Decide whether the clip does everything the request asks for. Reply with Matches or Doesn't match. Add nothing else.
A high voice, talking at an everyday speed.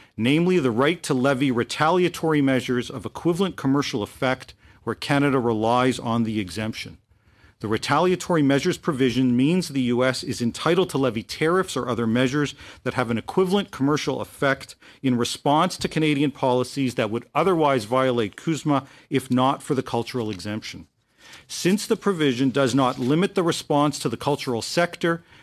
Doesn't match